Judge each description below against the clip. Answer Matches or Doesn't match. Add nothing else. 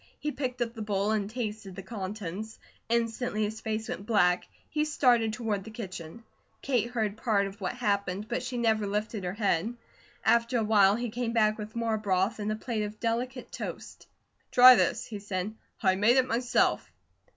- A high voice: Matches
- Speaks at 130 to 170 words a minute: Doesn't match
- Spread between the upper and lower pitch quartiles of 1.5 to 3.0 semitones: Matches